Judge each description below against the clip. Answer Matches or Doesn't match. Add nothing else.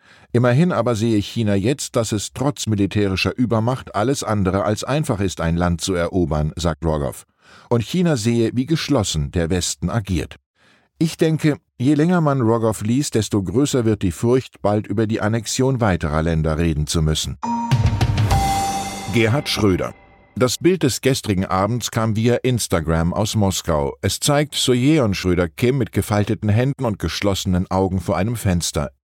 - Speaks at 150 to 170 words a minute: Matches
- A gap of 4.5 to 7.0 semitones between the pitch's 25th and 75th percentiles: Matches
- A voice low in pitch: Matches